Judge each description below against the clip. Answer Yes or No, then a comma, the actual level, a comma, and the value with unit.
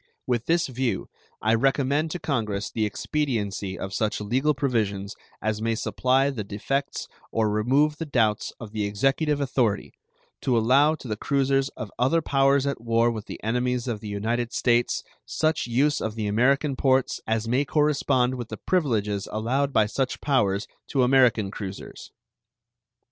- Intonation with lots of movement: No, average, 4.1 semitones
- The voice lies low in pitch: Yes, low, 125 Hz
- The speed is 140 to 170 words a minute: Yes, average, 160 wpm